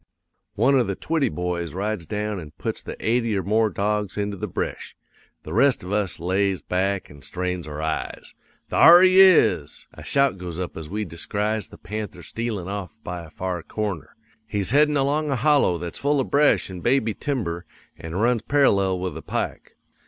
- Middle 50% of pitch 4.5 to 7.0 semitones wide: Yes, average, 5.2 semitones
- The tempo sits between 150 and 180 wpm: No, average, 190 wpm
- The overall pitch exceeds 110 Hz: No, low, 100 Hz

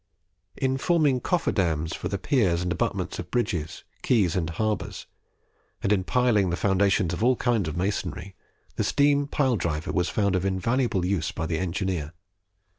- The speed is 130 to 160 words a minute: No, average, 170 wpm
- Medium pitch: No, very low, 95 Hz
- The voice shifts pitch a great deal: Yes, wide, 5.8 semitones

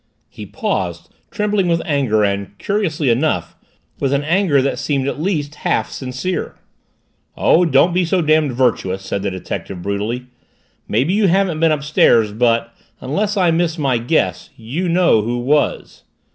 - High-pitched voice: No, medium, 140 Hz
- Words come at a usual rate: Yes, average, 155 wpm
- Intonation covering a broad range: Yes, wide, 6.6 semitones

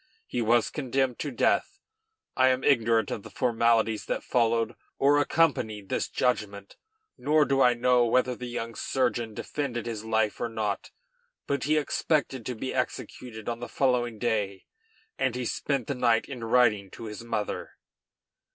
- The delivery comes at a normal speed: Yes, average, 160 wpm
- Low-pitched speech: Yes, low, 120 Hz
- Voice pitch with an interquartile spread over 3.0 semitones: No, narrow, 2.5 semitones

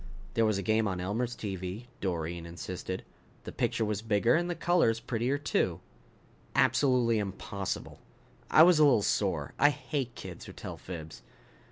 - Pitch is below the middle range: Yes, low, 110 Hz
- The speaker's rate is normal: Yes, average, 160 wpm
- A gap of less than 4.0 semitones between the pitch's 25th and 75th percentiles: No, average, 5.2 semitones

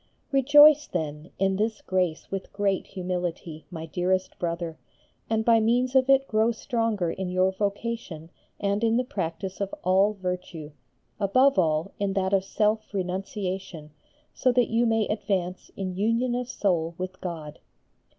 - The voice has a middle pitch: No, high, 195 Hz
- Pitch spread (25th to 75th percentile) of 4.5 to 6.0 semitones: No, average, 3.8 semitones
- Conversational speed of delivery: Yes, average, 150 wpm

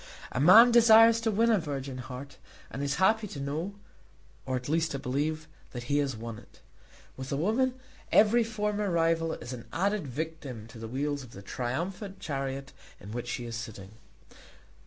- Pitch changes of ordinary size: No, wide, 7.8 semitones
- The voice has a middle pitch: Yes, medium, 145 Hz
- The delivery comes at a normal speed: Yes, average, 180 wpm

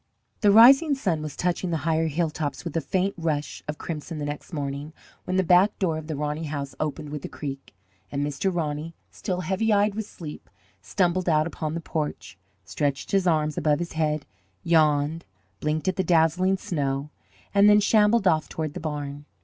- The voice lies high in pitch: No, medium, 160 Hz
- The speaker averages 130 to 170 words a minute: No, average, 190 wpm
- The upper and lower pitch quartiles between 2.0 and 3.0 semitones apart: No, average, 3.6 semitones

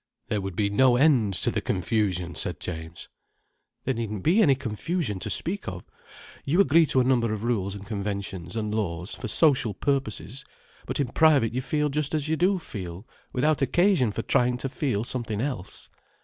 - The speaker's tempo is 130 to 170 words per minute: No, average, 185 wpm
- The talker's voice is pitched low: Yes, low, 120 Hz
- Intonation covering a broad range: Yes, wide, 6.0 semitones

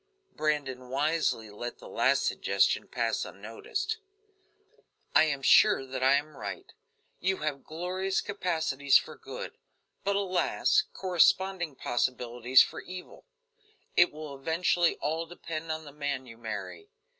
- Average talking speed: No, slow, 130 wpm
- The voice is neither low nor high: Yes, medium, 155 Hz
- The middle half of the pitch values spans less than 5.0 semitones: No, average, 5.3 semitones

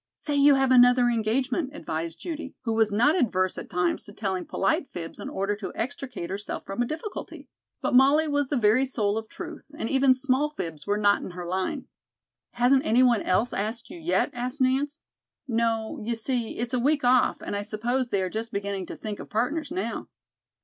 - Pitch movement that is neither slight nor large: Yes, average, 4.7 semitones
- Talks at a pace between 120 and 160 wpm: No, fast, 205 wpm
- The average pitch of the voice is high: Yes, high, 240 Hz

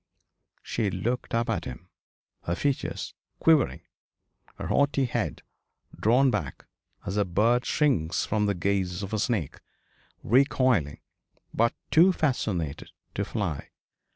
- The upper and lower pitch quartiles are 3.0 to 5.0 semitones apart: No, wide, 5.6 semitones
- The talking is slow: Yes, slow, 125 wpm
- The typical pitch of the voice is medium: No, low, 110 Hz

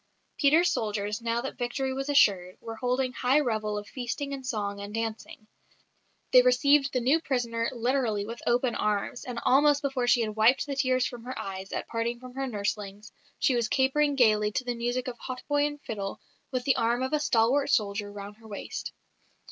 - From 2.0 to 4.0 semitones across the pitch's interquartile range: Yes, average, 3.6 semitones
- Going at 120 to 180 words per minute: No, average, 195 wpm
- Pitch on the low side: No, high, 245 Hz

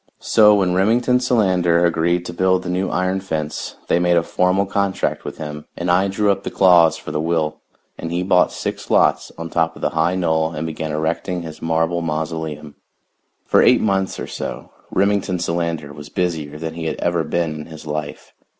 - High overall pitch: No, very low, 85 Hz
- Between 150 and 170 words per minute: No, average, 195 wpm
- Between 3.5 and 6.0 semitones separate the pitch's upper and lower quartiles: No, narrow, 2.6 semitones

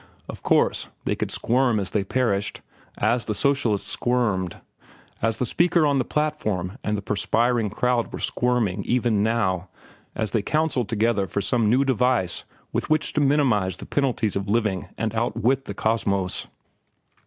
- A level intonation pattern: No, average, 3.7 semitones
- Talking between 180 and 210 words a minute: No, average, 160 wpm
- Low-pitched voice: Yes, low, 115 Hz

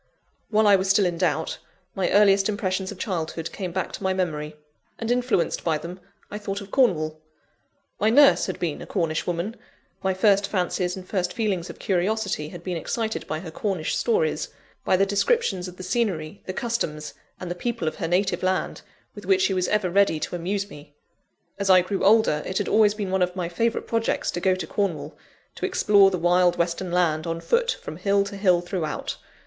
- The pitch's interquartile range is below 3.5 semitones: Yes, average, 2.9 semitones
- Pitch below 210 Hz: Yes, medium, 185 Hz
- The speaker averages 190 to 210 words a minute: Yes, fast, 205 wpm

